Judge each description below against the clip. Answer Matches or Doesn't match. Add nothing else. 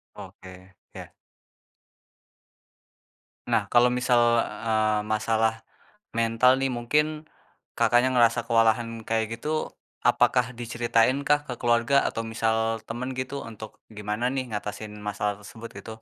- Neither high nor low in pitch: Doesn't match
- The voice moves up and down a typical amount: Doesn't match